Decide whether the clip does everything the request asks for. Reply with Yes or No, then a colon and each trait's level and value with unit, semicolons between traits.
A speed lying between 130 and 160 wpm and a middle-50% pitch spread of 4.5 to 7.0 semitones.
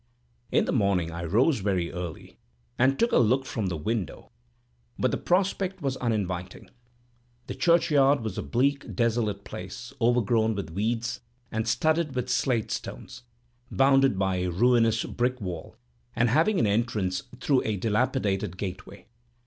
Yes: average, 150 wpm; average, 5.2 semitones